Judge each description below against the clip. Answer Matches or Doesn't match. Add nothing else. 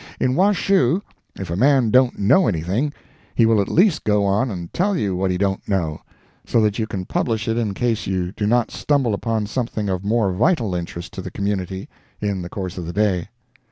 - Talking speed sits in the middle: Doesn't match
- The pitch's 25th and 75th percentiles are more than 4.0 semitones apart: Matches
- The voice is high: Doesn't match